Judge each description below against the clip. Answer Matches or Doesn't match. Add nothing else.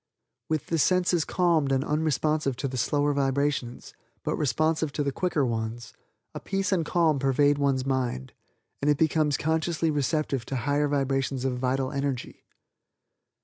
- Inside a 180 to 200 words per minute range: Doesn't match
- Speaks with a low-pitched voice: Doesn't match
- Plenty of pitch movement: Doesn't match